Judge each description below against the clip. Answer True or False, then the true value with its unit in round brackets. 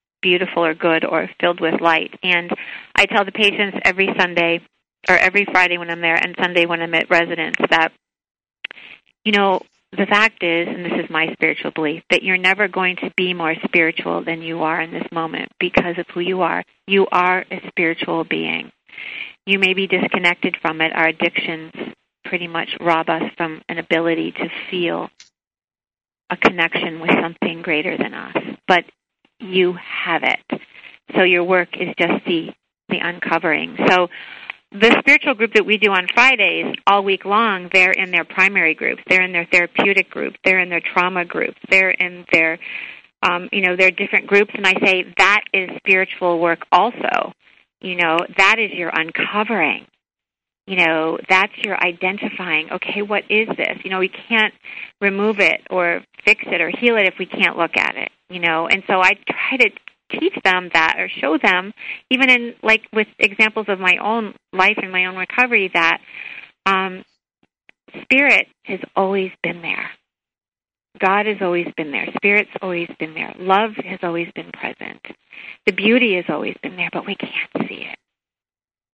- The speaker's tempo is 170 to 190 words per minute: True (175 wpm)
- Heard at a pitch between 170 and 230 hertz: True (185 Hz)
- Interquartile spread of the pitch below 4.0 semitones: True (2.9 semitones)